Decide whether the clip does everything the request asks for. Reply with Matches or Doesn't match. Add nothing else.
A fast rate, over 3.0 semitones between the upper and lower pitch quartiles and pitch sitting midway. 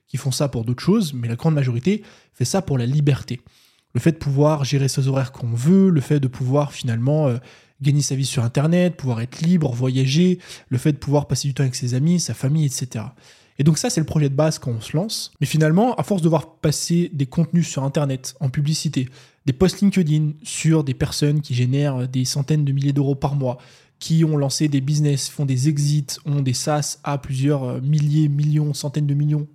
Doesn't match